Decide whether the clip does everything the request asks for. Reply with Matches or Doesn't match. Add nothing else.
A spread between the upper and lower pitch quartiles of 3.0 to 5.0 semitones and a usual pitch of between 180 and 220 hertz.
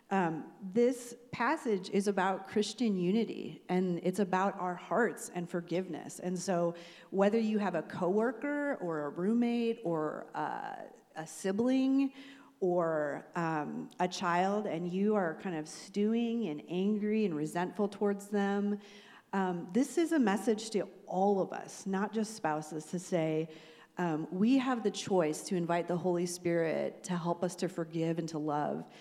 Matches